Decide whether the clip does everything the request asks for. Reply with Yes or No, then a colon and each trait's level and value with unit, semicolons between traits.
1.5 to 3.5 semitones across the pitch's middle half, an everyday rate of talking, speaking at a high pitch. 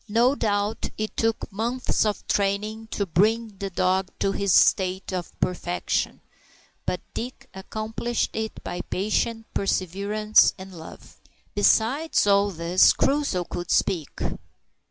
No: average, 2.9 semitones; slow, 130 wpm; high, 205 Hz